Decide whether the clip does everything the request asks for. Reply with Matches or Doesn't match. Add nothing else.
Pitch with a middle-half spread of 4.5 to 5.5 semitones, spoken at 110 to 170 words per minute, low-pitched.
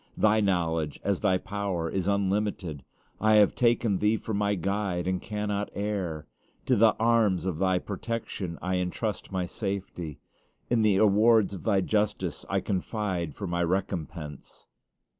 Doesn't match